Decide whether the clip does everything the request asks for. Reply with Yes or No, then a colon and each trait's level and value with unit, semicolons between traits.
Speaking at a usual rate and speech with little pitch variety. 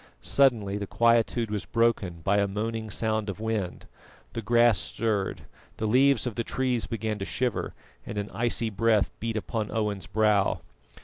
Yes: average, 165 wpm; narrow, 2.3 semitones